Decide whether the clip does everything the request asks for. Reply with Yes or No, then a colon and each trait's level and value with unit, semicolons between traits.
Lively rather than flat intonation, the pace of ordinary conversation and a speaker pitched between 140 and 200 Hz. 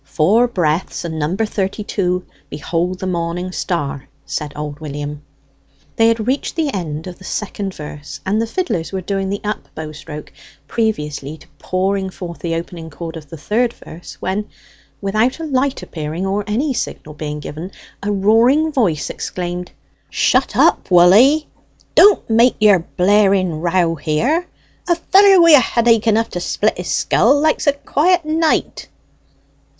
Yes: wide, 5.8 semitones; average, 160 wpm; high, 190 Hz